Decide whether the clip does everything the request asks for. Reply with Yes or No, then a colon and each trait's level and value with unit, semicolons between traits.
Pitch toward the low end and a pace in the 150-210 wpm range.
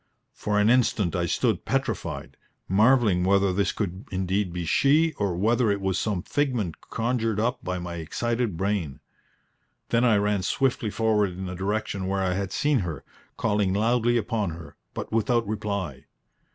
Yes: low, 100 Hz; average, 165 wpm